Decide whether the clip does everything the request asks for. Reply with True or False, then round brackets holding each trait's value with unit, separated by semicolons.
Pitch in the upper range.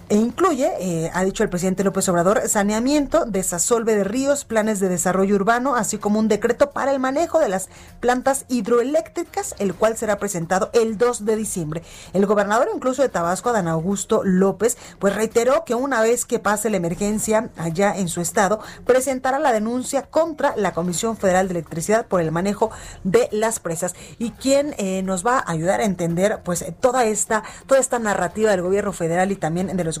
True (215 Hz)